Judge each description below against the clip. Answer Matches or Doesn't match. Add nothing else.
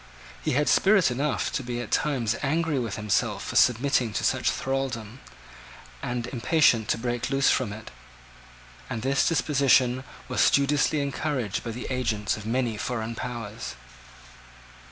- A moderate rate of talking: Matches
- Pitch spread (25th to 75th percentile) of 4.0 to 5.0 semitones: Doesn't match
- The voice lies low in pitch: Matches